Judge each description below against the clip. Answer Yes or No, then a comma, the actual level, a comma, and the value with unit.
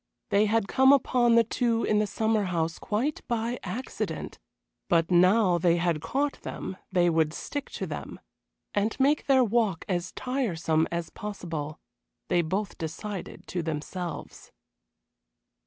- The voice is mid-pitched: No, high, 195 Hz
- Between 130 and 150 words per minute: Yes, average, 140 wpm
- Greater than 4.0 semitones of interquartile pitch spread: Yes, average, 5.3 semitones